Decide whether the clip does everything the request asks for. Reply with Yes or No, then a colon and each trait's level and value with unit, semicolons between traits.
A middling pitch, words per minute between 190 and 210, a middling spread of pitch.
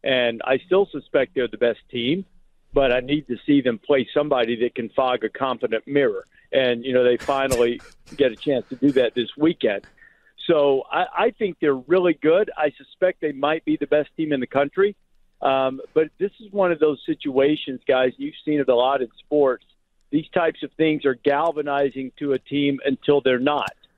Yes: medium, 145 Hz; fast, 205 wpm; average, 3.0 semitones